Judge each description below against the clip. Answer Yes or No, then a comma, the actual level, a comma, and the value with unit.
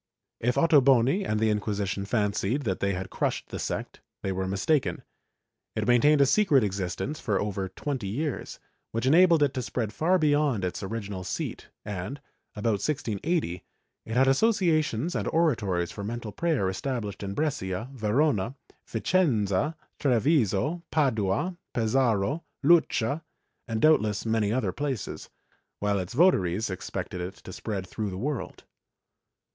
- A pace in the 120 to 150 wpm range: Yes, average, 140 wpm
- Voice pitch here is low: Yes, low, 115 Hz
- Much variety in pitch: Yes, wide, 6.6 semitones